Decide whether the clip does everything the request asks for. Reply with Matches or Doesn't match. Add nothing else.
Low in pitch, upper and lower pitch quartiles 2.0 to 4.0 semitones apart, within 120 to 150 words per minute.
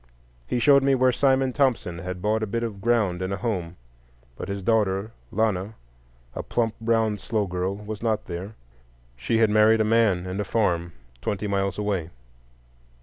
Doesn't match